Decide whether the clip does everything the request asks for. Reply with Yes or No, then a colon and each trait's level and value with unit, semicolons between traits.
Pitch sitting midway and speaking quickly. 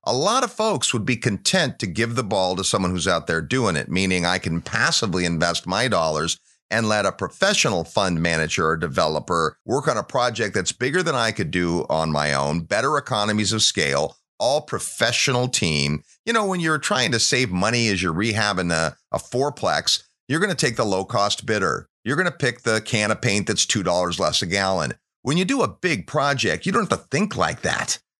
No: low, 105 Hz; fast, 215 wpm